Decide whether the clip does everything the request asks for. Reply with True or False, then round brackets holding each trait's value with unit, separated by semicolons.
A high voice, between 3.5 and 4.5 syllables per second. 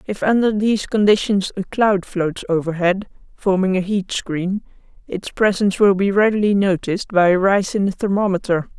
False (195 Hz; 5.1 syllables/s)